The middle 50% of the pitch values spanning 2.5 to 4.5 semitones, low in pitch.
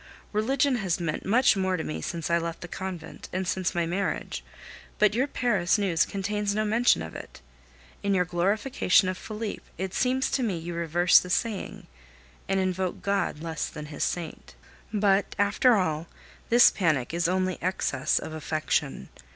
No: average, 3.6 semitones; medium, 185 Hz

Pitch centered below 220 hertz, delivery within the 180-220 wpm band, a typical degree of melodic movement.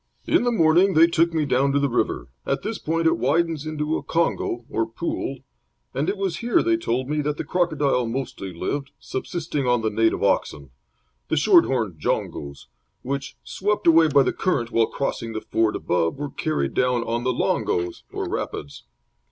No: medium, 140 Hz; average, 185 wpm; wide, 6.1 semitones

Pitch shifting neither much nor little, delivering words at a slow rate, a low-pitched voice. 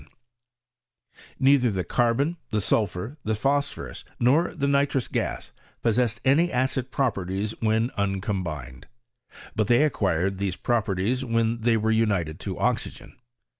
Yes: average, 4.9 semitones; slow, 125 wpm; low, 115 Hz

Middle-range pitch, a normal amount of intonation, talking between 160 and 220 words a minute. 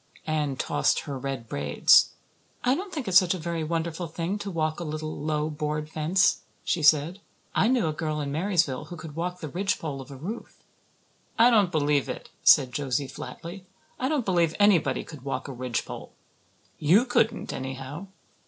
Yes: medium, 155 Hz; average, 4.2 semitones; average, 180 wpm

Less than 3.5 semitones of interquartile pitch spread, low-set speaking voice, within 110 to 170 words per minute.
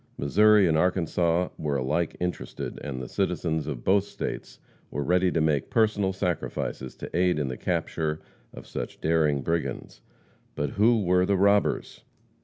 No: average, 3.9 semitones; very low, 85 Hz; average, 155 wpm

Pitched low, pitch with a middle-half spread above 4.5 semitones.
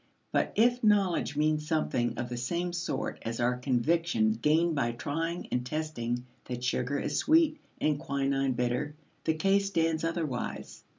No: medium, 150 Hz; wide, 5.4 semitones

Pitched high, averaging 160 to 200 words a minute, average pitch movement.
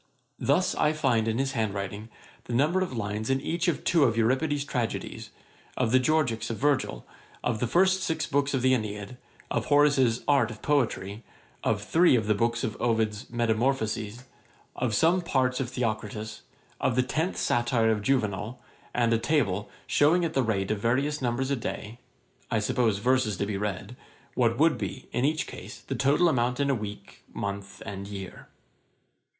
No: low, 120 Hz; average, 180 wpm; average, 4.3 semitones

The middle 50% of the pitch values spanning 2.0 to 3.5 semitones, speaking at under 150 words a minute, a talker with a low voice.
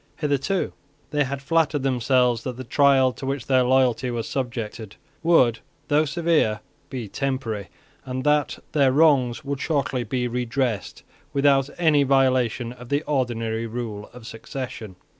Yes: average, 2.9 semitones; average, 140 wpm; low, 130 Hz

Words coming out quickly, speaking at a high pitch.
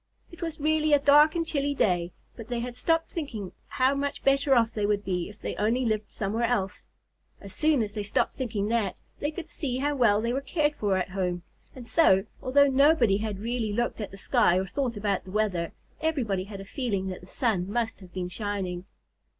Yes: fast, 215 wpm; high, 225 Hz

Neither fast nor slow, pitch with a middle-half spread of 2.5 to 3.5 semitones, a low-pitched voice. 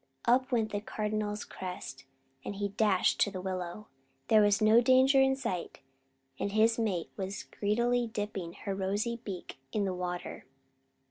No: average, 155 wpm; average, 3.2 semitones; high, 205 Hz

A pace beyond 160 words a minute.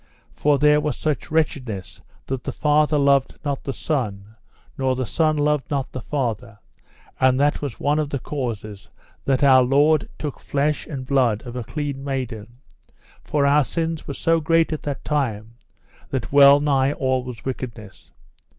Yes: average, 170 wpm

